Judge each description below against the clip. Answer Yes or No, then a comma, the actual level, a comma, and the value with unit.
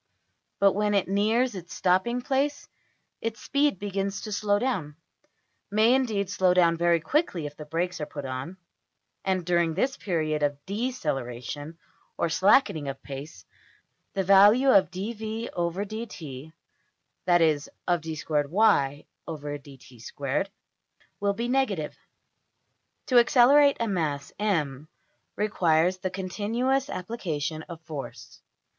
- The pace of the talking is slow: Yes, slow, 115 wpm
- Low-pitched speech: No, medium, 185 Hz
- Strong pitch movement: Yes, wide, 5.8 semitones